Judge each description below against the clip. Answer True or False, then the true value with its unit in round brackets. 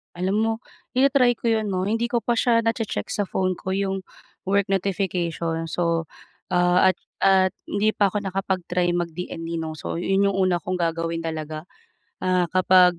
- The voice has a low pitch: False (185 Hz)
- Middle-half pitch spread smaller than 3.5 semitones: True (2.7 semitones)